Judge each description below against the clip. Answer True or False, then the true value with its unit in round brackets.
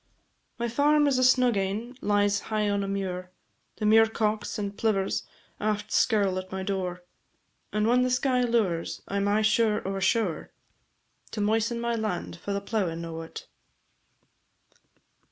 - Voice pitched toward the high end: True (210 Hz)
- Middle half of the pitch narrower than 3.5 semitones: True (2.9 semitones)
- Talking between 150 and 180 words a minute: True (155 wpm)